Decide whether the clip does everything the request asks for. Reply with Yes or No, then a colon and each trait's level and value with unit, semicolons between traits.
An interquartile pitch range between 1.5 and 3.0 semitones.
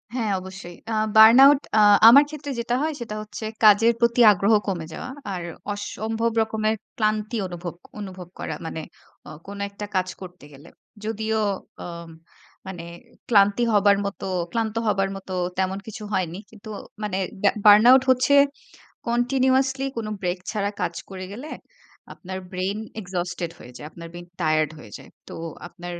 No: average, 3.8 semitones